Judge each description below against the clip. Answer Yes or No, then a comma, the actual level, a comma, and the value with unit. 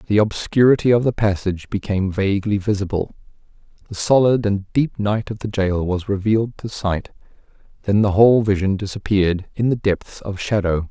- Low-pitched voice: Yes, low, 100 Hz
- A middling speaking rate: Yes, average, 165 wpm